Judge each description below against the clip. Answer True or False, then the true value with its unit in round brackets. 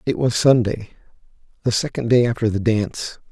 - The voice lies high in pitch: False (115 Hz)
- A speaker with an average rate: True (165 wpm)